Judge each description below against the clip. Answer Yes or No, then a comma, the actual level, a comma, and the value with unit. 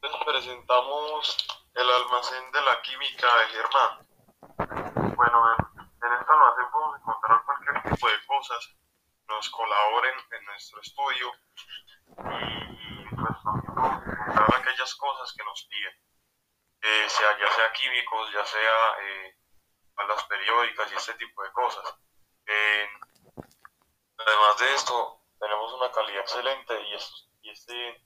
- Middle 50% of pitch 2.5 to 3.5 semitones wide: Yes, average, 2.9 semitones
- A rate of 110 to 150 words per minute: Yes, average, 130 wpm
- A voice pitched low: Yes, low, 115 Hz